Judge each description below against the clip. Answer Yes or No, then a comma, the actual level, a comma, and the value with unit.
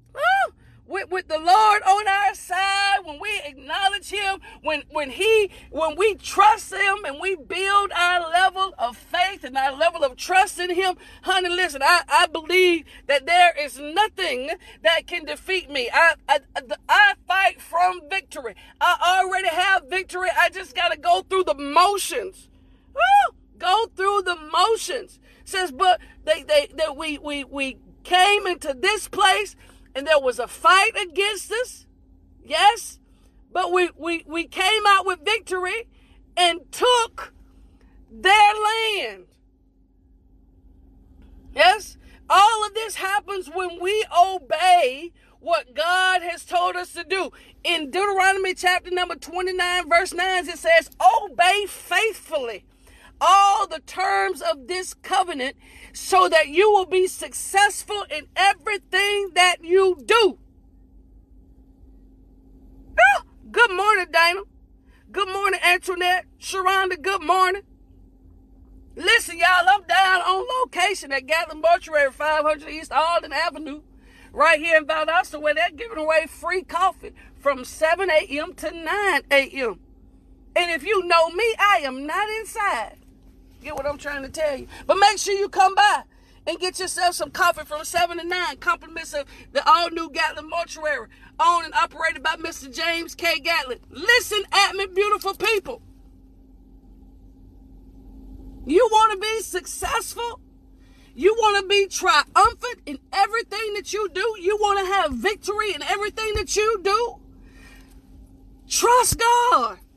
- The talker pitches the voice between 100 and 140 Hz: No, very high, 360 Hz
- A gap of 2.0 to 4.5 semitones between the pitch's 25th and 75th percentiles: Yes, average, 4.0 semitones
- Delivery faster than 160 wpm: No, average, 140 wpm